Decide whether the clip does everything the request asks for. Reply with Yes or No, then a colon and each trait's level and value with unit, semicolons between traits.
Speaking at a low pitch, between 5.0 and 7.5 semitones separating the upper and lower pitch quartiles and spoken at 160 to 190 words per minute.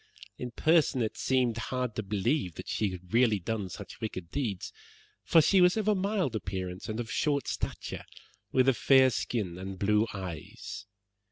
Yes: low, 115 Hz; wide, 5.6 semitones; average, 175 wpm